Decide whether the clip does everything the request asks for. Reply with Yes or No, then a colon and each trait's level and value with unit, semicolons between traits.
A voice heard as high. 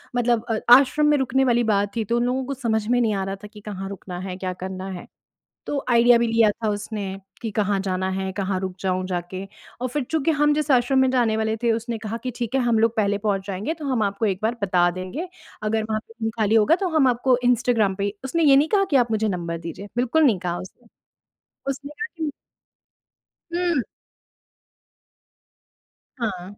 Yes: high, 225 Hz